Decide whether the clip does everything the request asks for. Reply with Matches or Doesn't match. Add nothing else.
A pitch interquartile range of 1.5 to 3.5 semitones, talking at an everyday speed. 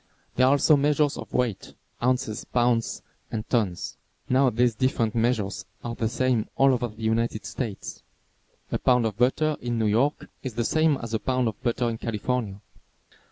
Matches